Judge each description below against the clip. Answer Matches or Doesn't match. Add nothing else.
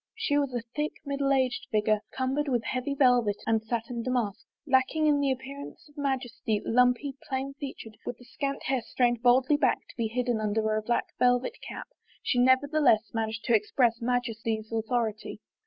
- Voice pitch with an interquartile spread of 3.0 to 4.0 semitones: Matches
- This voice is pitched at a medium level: Doesn't match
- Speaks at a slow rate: Doesn't match